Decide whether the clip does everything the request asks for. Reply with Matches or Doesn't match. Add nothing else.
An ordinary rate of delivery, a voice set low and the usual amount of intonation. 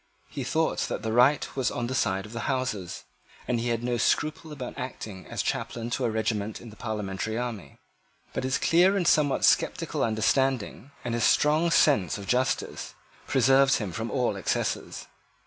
Matches